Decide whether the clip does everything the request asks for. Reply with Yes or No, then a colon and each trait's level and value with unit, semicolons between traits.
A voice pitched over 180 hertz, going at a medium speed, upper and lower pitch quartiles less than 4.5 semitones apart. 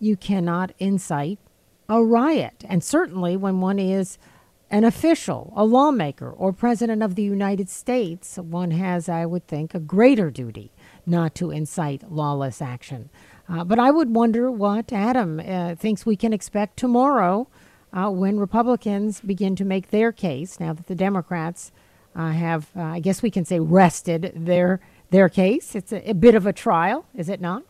Yes: high, 190 Hz; average, 175 wpm; average, 4.1 semitones